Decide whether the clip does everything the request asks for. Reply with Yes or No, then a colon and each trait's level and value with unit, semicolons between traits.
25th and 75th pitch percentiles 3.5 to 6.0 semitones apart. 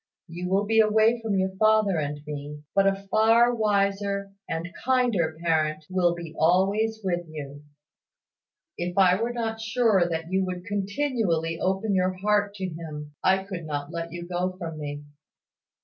Yes: average, 4.2 semitones